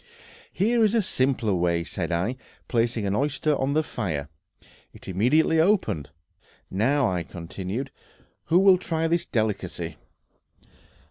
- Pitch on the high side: No, low, 120 Hz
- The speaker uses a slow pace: Yes, slow, 130 wpm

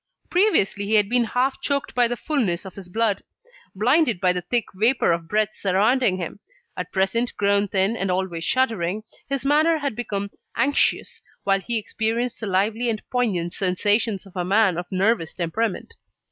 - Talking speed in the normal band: Yes, average, 175 wpm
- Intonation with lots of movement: No, average, 4.3 semitones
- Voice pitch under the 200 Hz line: No, high, 210 Hz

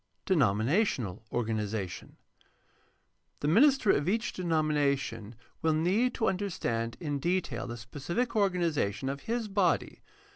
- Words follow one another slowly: Yes, slow, 125 wpm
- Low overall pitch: No, medium, 155 Hz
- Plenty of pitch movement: Yes, wide, 8.7 semitones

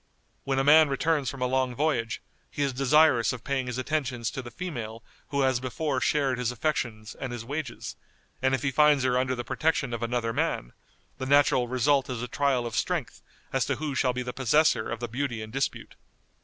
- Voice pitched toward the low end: Yes, low, 130 Hz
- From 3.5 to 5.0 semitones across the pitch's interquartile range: No, average, 2.8 semitones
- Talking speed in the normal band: No, fast, 210 wpm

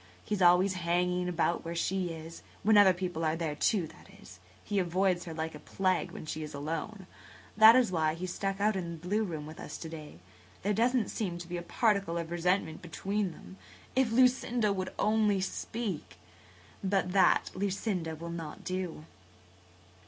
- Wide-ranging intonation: No, average, 3.3 semitones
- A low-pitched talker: No, medium, 180 Hz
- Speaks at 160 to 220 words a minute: Yes, average, 180 wpm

